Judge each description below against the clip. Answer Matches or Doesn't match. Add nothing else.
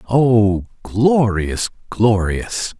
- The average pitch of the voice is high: Doesn't match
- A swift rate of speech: Doesn't match